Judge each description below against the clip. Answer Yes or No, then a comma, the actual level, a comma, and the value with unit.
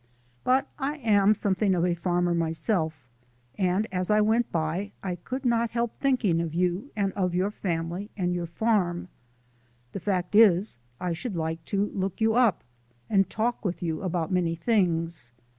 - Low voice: No, medium, 185 Hz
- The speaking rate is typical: Yes, average, 165 wpm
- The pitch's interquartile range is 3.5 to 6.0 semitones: Yes, average, 4.1 semitones